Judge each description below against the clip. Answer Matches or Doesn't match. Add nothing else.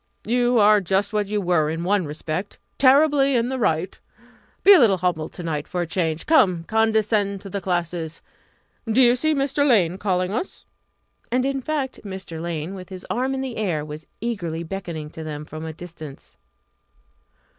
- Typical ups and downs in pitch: Doesn't match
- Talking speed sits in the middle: Matches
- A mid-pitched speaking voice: Doesn't match